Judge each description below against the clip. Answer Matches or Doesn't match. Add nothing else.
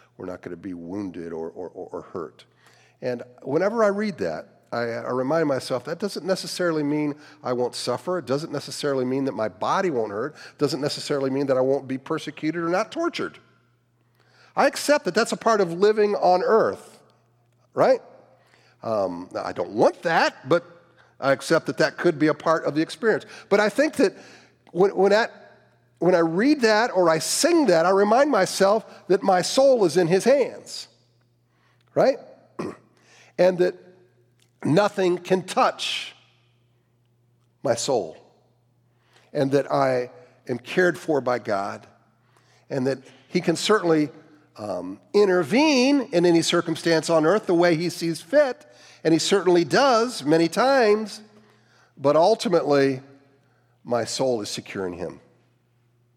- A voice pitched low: Doesn't match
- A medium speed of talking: Matches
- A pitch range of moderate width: Doesn't match